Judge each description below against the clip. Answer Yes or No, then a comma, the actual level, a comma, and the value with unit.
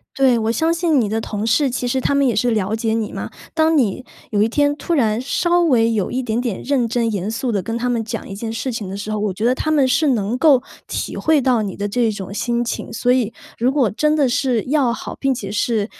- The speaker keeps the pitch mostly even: No, average, 3.7 semitones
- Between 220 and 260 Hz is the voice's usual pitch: Yes, high, 235 Hz